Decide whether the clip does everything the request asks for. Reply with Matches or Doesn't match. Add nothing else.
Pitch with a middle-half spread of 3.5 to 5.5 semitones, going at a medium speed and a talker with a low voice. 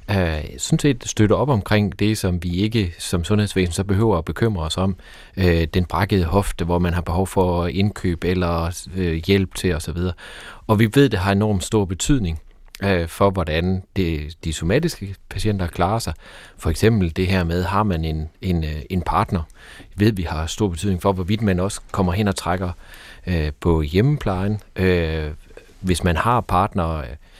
Doesn't match